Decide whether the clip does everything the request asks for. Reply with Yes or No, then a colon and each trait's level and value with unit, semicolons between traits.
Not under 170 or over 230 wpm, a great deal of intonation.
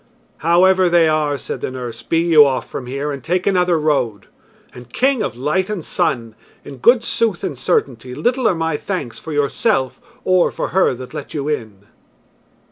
Yes: average, 185 wpm; wide, 5.9 semitones